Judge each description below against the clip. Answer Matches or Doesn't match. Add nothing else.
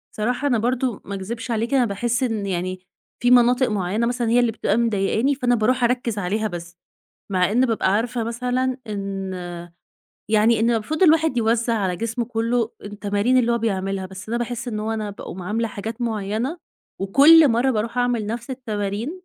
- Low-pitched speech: Doesn't match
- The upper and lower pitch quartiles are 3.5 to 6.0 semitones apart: Doesn't match